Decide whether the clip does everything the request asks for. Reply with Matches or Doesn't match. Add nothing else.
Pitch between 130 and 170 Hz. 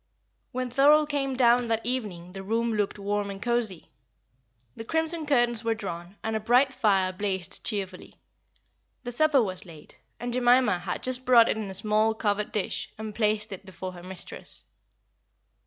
Doesn't match